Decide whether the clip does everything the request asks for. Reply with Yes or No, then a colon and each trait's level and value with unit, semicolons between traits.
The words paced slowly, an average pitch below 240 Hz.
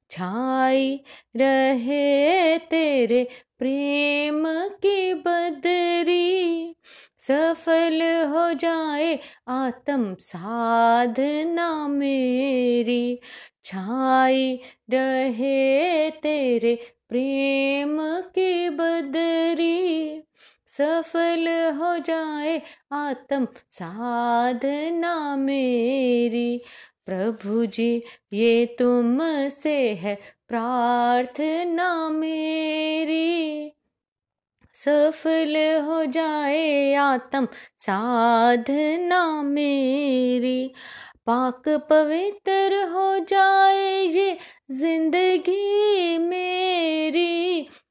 No: slow, 55 wpm; very high, 295 Hz